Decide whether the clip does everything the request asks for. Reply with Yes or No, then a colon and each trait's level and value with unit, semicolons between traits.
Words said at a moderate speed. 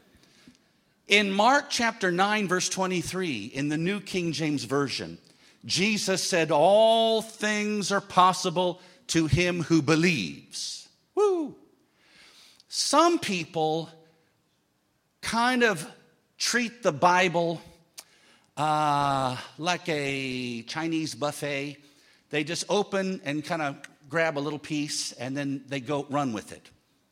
No: slow, 115 wpm